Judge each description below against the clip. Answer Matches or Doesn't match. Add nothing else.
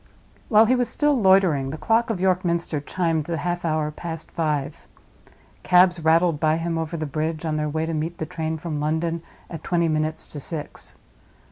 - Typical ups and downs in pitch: Doesn't match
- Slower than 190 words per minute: Doesn't match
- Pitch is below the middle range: Doesn't match